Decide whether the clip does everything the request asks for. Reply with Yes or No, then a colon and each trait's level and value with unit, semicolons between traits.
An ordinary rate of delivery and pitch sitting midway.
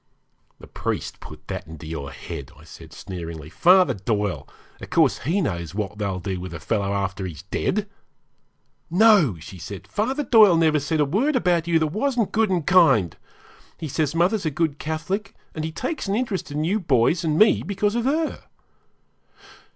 Yes: average, 180 wpm; medium, 160 Hz